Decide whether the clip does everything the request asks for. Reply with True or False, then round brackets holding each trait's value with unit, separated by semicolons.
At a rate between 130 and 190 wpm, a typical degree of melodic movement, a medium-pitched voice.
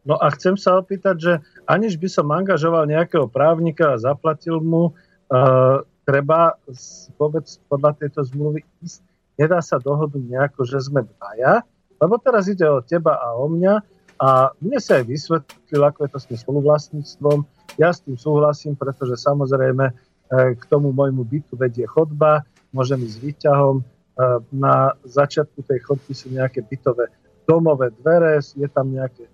True (160 wpm; 3.4 semitones; 145 Hz)